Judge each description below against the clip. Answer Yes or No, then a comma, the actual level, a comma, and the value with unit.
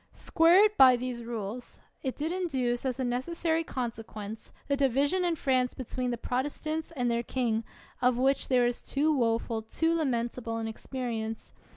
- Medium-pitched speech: No, very high, 255 Hz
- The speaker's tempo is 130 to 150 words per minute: No, average, 170 wpm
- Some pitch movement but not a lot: Yes, average, 3.7 semitones